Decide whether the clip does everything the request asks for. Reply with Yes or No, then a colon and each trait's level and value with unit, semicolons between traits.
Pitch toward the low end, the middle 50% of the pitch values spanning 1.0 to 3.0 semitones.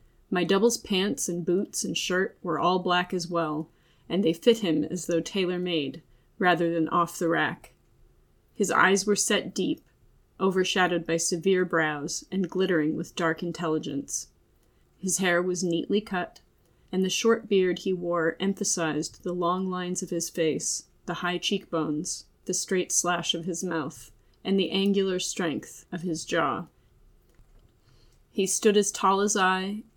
No: medium, 180 Hz; narrow, 2.4 semitones